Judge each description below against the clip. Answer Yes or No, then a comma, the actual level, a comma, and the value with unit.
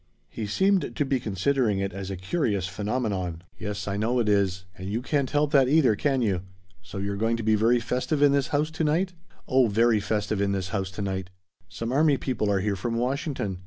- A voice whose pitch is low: Yes, low, 110 Hz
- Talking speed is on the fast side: Yes, fast, 220 wpm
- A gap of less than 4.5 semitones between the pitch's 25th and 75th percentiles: No, average, 5.3 semitones